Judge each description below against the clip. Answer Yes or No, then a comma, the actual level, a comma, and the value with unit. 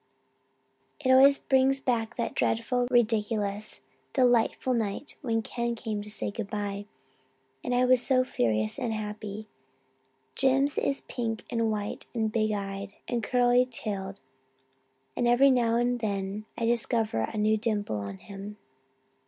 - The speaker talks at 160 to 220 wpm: No, average, 145 wpm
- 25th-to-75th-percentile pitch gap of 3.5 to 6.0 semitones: No, average, 3.0 semitones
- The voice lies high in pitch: Yes, high, 225 Hz